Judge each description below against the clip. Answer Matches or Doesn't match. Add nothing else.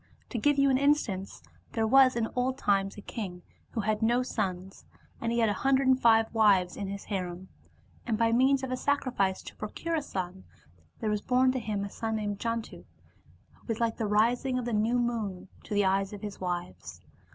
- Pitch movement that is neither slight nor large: Matches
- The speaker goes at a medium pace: Doesn't match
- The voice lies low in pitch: Doesn't match